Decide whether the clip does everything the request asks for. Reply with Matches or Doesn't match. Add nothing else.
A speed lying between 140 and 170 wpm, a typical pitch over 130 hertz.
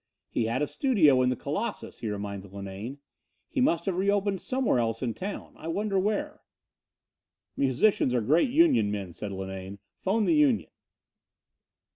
Matches